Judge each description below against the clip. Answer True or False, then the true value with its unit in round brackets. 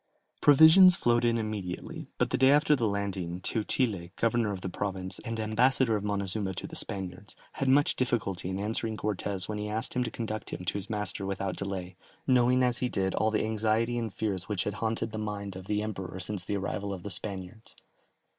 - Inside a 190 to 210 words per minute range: True (205 wpm)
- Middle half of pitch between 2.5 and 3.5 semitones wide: True (3.1 semitones)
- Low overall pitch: True (105 Hz)